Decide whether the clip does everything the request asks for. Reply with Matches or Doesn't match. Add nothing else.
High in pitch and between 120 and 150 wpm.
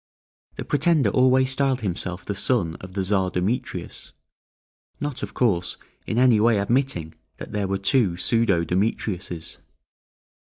Doesn't match